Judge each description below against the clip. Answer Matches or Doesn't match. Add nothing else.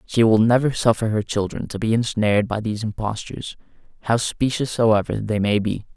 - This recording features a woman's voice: Doesn't match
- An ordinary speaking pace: Matches